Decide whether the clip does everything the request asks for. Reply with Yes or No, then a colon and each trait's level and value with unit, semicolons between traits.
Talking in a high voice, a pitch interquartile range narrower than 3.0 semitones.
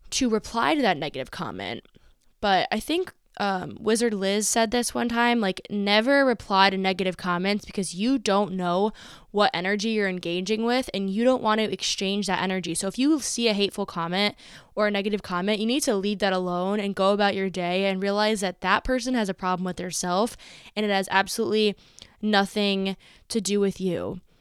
Yes: high, 200 Hz; narrow, 2.6 semitones